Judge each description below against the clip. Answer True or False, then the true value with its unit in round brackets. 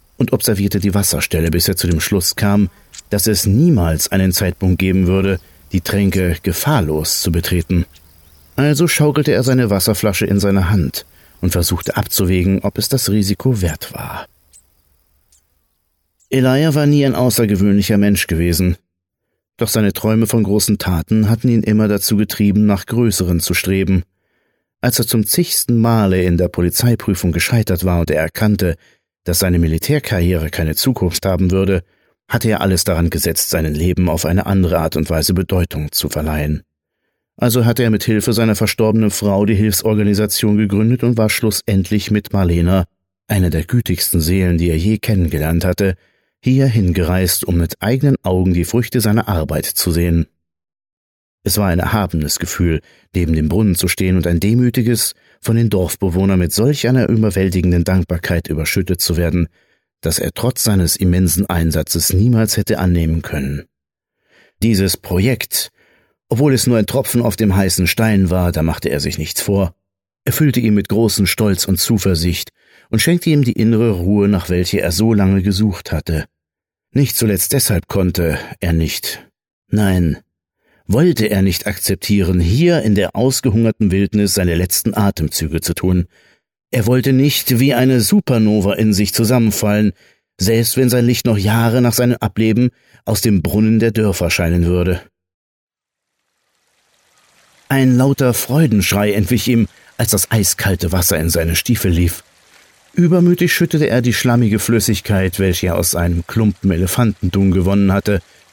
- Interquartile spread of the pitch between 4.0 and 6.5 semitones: True (4.3 semitones)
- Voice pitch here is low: True (100 Hz)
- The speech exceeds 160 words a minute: False (155 wpm)